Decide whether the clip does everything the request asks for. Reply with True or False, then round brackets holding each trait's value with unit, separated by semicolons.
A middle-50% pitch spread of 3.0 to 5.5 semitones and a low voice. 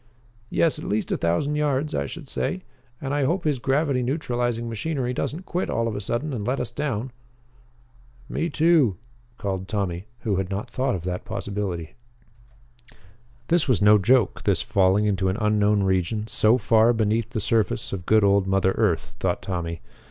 True (5.2 semitones; 110 Hz)